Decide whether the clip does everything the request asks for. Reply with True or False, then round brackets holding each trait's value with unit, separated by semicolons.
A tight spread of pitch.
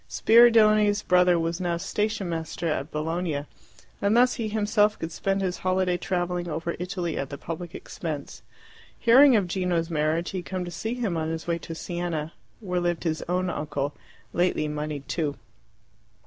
False (3.2 semitones)